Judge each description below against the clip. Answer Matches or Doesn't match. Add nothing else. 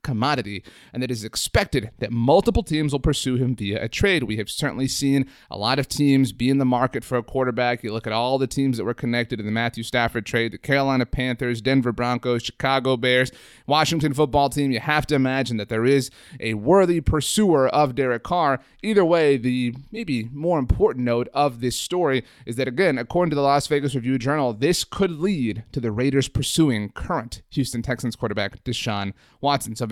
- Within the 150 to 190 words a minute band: Doesn't match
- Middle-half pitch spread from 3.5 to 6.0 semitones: Doesn't match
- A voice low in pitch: Matches